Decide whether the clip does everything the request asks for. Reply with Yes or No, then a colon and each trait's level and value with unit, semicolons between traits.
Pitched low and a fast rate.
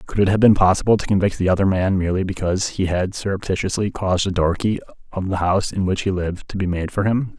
Yes: very low, 95 Hz; fast, 250 wpm